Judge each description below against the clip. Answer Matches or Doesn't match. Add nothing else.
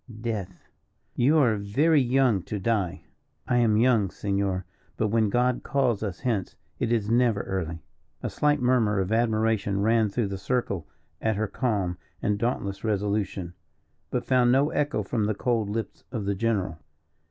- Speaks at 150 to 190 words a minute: Matches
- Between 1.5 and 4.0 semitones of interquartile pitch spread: Matches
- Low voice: Matches